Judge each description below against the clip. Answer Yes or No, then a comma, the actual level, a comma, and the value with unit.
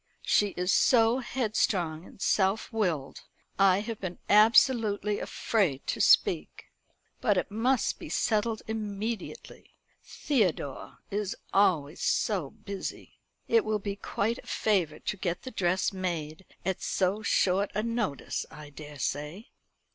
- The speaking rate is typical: No, slow, 130 wpm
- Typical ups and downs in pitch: Yes, average, 3.8 semitones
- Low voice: No, high, 200 Hz